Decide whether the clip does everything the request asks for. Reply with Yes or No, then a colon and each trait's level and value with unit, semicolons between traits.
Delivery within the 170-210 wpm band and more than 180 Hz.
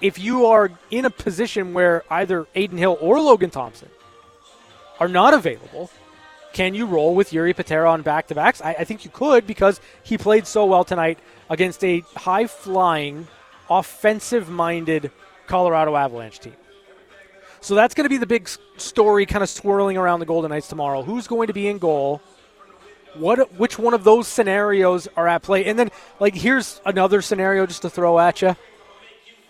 Yes: average, 180 wpm; high, 190 Hz